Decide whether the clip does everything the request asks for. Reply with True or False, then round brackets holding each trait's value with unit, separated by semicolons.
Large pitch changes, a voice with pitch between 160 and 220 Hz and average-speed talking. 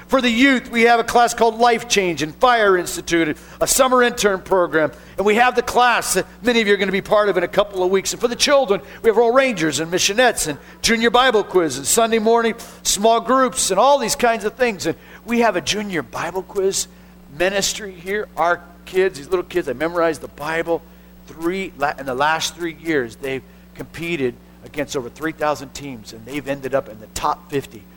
False (6.4 semitones; 185 Hz; 215 wpm)